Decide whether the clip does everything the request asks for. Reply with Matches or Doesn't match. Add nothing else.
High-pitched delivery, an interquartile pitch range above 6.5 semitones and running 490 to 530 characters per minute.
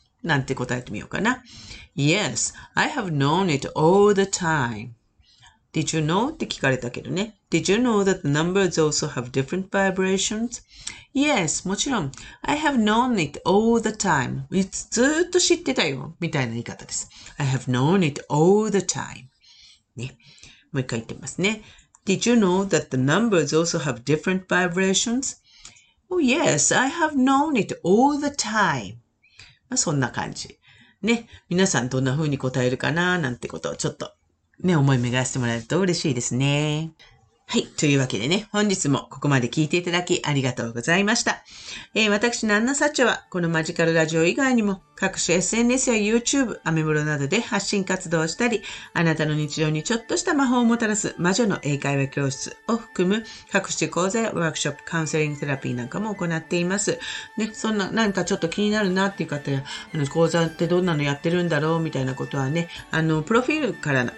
Doesn't match